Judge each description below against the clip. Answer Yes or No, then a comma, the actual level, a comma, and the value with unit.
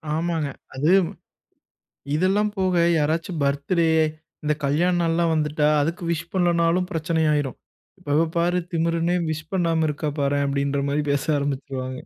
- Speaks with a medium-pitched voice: Yes, medium, 160 Hz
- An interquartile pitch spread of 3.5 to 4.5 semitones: No, average, 3.0 semitones